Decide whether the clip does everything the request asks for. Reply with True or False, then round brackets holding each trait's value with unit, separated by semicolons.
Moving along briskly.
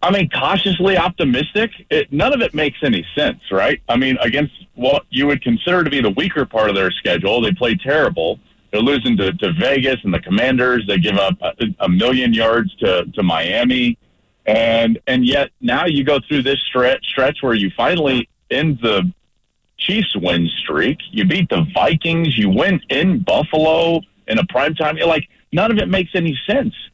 False (190 wpm)